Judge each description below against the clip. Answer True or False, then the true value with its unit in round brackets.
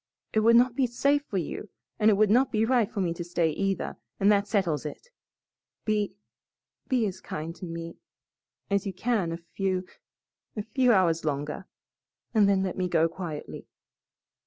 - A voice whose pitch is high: True (195 Hz)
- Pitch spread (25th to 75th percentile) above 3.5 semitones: True (4.5 semitones)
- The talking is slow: False (180 wpm)